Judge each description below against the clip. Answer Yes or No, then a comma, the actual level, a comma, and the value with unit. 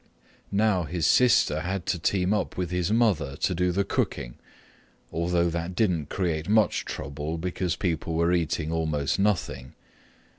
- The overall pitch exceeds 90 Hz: No, very low, 85 Hz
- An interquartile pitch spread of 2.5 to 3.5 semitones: Yes, average, 3.0 semitones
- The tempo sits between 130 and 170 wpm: Yes, average, 150 wpm